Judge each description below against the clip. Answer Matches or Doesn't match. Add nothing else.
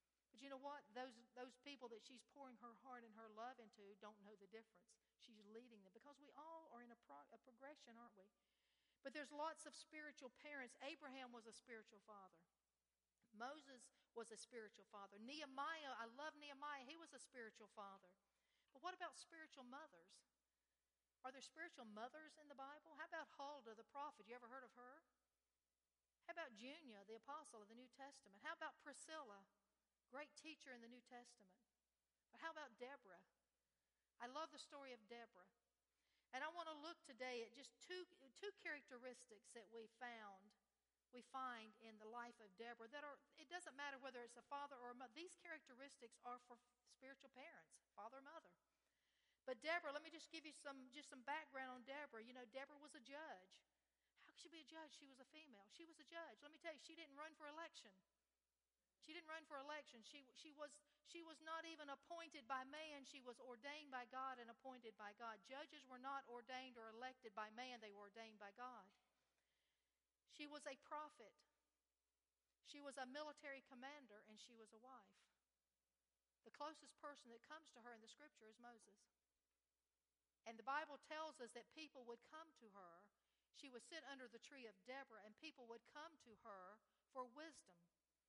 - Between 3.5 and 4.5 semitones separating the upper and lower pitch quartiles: Doesn't match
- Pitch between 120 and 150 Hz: Doesn't match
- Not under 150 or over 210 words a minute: Matches